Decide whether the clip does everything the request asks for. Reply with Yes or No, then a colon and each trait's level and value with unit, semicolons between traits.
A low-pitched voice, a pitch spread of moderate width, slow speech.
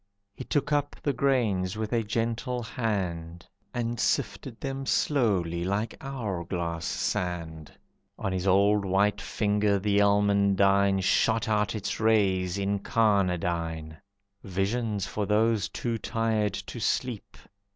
Yes: low, 100 Hz; average, 3.4 semitones; slow, 120 wpm